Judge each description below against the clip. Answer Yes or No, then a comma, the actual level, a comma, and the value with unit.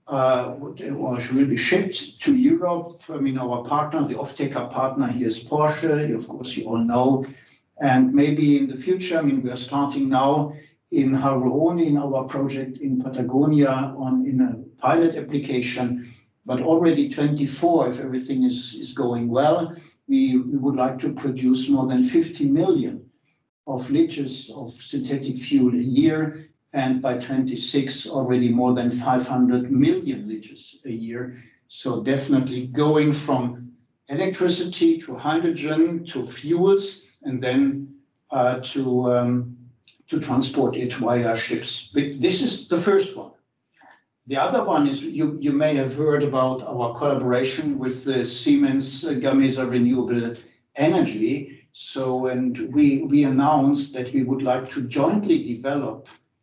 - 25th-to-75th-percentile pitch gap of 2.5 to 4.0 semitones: Yes, average, 3.2 semitones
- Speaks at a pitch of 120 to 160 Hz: Yes, low, 135 Hz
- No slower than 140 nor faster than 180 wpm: Yes, average, 145 wpm